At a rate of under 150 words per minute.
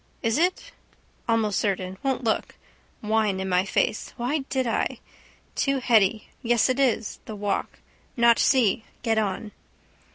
Yes: average, 140 wpm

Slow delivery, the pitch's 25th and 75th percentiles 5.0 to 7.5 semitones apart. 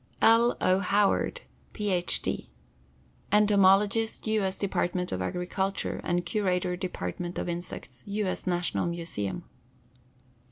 No: slow, 115 wpm; narrow, 2.6 semitones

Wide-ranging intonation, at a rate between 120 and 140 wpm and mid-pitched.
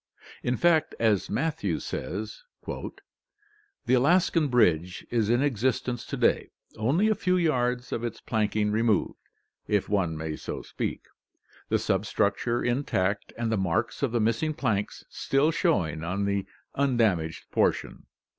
No: wide, 6.1 semitones; slow, 135 wpm; low, 120 Hz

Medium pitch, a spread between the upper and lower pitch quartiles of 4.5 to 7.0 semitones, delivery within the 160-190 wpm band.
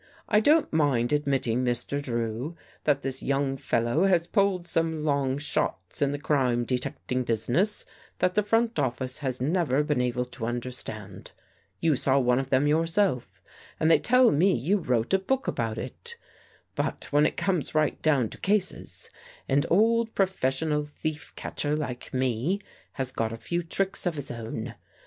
Yes: medium, 145 Hz; wide, 5.5 semitones; average, 170 wpm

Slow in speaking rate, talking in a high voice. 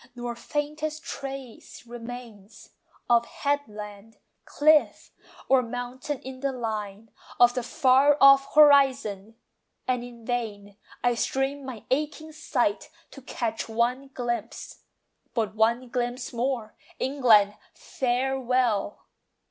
Yes: slow, 110 wpm; high, 245 Hz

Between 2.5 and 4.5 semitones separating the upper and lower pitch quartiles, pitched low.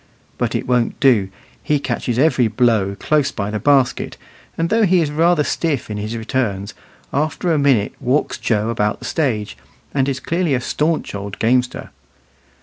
No: wide, 5.6 semitones; low, 130 Hz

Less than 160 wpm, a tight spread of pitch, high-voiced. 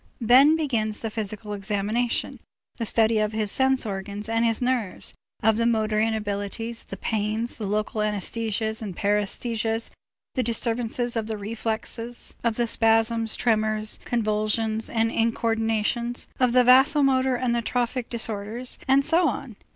Yes: average, 140 wpm; narrow, 2.0 semitones; high, 225 Hz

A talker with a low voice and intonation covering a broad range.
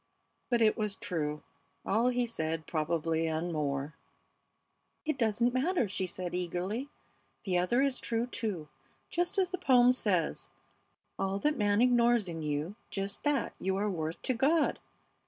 No: high, 205 Hz; wide, 6.7 semitones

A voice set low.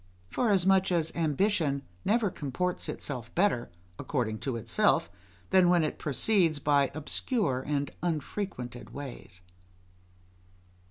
No: medium, 155 Hz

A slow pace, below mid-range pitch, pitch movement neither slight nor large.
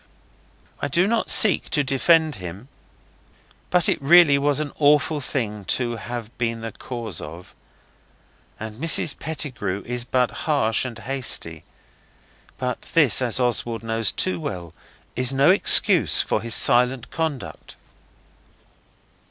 Yes: slow, 130 wpm; low, 125 Hz; average, 4.5 semitones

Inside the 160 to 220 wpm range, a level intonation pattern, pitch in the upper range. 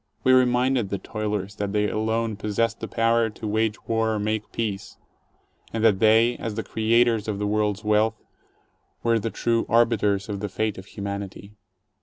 No: average, 185 wpm; narrow, 1.8 semitones; low, 110 Hz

